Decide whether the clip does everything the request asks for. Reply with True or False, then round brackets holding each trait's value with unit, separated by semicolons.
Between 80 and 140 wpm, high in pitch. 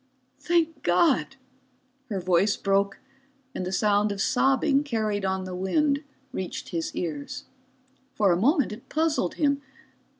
True (135 wpm; 205 Hz)